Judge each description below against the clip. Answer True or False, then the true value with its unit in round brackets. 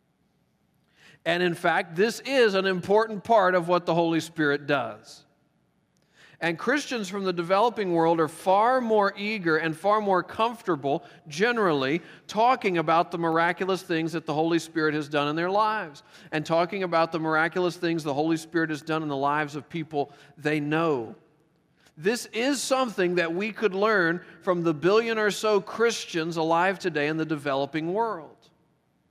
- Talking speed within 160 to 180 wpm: True (165 wpm)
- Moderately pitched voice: True (170 Hz)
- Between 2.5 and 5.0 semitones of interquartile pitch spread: True (4.5 semitones)